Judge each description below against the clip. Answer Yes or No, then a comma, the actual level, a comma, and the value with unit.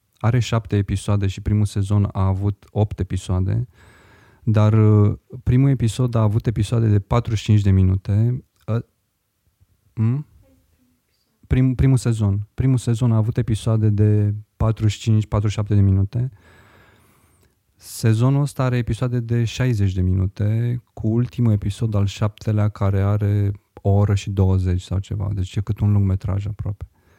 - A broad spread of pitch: No, narrow, 2.5 semitones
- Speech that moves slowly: No, average, 130 wpm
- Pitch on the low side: Yes, low, 105 Hz